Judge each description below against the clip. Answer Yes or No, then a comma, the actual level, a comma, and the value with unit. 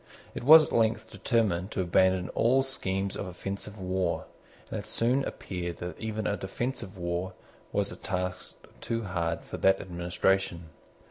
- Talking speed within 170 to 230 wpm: No, average, 155 wpm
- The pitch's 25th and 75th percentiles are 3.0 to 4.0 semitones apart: Yes, average, 3.7 semitones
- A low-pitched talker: Yes, very low, 95 Hz